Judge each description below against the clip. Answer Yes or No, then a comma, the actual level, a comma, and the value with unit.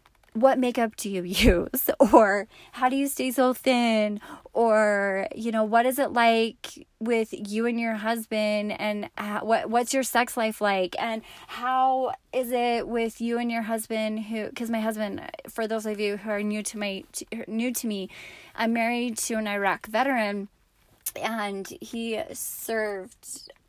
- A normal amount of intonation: No, narrow, 2.2 semitones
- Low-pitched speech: No, high, 225 Hz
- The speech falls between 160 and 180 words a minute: Yes, average, 165 wpm